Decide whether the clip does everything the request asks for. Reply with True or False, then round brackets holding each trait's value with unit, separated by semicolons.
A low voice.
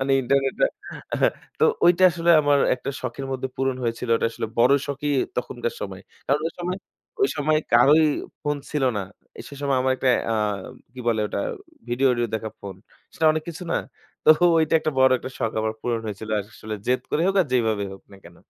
True (130 Hz)